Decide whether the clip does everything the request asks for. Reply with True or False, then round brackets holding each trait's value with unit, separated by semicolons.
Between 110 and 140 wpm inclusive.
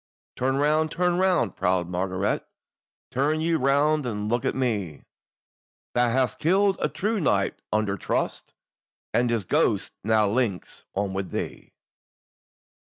True (135 wpm)